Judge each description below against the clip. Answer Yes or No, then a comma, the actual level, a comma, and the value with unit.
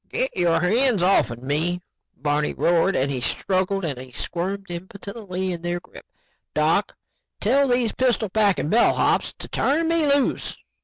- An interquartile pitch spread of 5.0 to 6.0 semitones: Yes, wide, 5.5 semitones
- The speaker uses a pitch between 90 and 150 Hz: No, high, 190 Hz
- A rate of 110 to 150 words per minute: Yes, average, 145 wpm